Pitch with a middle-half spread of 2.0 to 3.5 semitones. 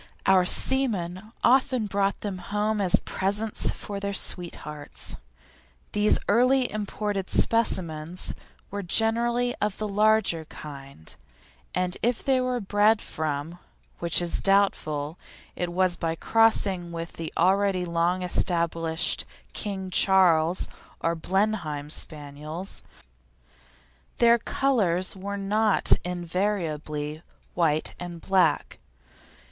No: average, 4.0 semitones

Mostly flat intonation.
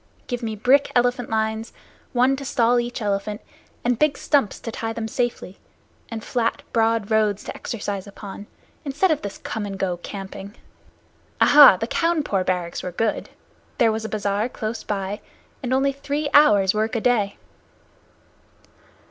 No: average, 3.4 semitones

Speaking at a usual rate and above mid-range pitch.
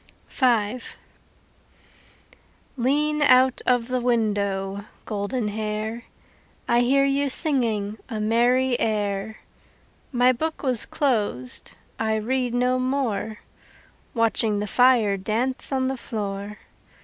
No: slow, 100 wpm; high, 235 Hz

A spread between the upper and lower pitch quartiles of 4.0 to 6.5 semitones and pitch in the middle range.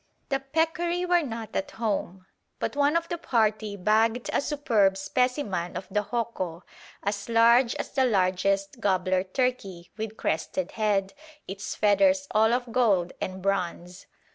No: average, 4.8 semitones; high, 215 Hz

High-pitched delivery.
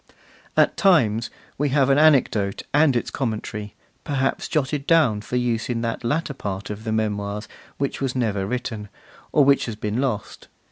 No: low, 120 Hz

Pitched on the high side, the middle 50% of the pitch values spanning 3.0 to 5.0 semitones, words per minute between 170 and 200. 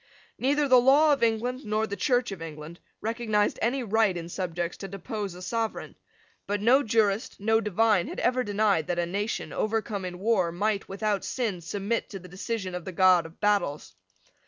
Yes: high, 205 Hz; average, 3.9 semitones; average, 185 wpm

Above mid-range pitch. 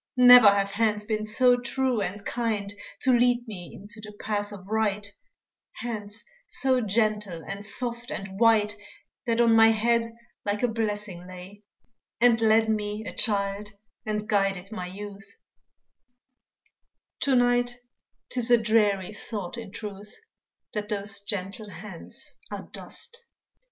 Yes: high, 210 Hz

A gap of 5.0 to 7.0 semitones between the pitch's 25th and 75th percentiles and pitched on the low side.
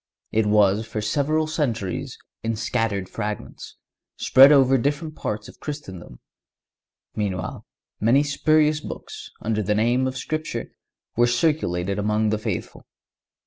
Yes: wide, 5.5 semitones; low, 115 Hz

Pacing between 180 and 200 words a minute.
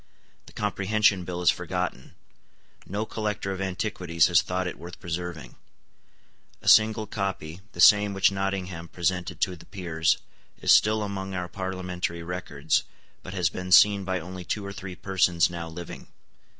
No: average, 155 wpm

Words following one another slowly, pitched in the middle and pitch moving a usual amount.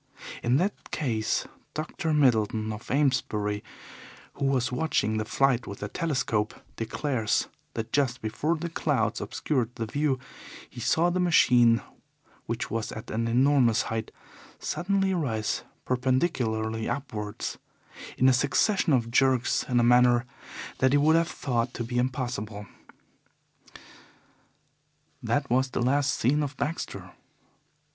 No: slow, 130 wpm; low, 125 Hz; average, 4.3 semitones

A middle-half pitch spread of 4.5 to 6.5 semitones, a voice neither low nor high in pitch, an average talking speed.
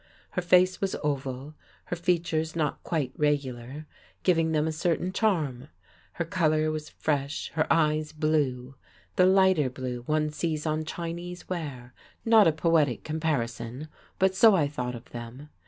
No: average, 3.5 semitones; medium, 155 Hz; average, 150 wpm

